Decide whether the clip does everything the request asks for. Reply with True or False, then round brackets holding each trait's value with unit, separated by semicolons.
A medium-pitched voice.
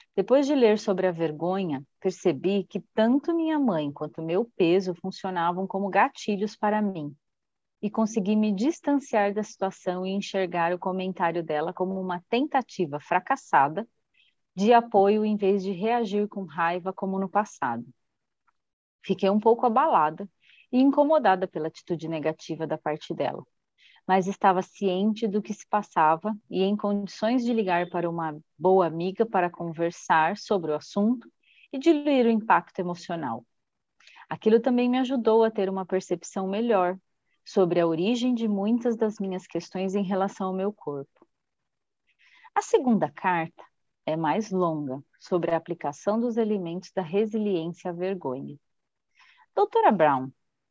False (195 Hz)